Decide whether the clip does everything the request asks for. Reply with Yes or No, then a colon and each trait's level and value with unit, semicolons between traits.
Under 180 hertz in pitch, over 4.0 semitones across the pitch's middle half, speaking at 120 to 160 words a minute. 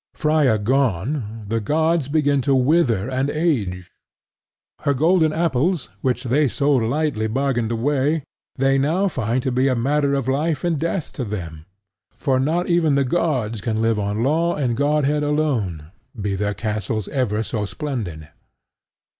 Yes: low, 135 Hz; average, 5.2 semitones; average, 155 wpm